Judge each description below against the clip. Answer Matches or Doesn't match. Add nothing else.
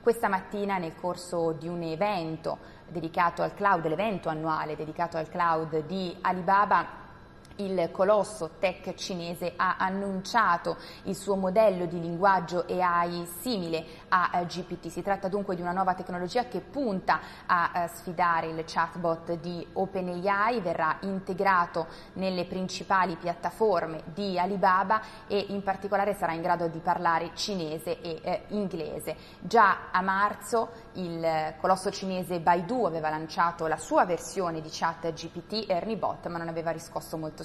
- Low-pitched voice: Doesn't match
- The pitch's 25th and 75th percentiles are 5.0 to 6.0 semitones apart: Doesn't match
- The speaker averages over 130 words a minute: Matches